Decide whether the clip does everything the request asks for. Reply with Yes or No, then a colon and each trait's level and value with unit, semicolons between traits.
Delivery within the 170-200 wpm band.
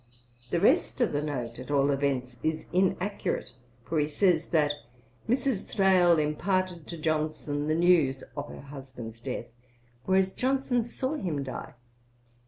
No: average, 145 wpm